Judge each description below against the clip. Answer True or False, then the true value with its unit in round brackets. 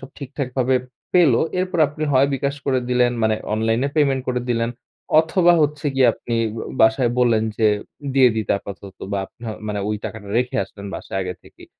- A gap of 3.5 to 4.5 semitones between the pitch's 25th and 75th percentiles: True (4.0 semitones)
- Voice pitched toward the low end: True (125 Hz)